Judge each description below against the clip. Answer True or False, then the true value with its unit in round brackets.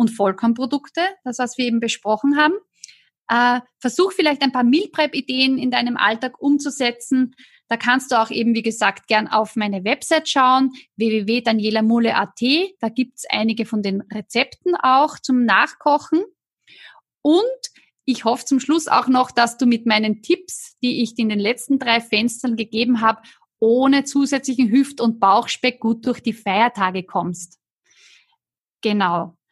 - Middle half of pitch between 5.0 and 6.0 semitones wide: False (3.4 semitones)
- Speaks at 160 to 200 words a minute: False (150 wpm)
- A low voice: False (245 Hz)